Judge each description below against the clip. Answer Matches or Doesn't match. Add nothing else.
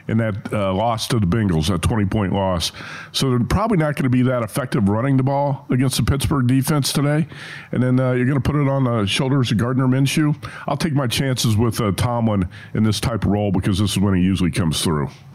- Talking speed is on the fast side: Matches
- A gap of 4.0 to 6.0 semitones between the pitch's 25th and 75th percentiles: Matches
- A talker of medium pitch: Doesn't match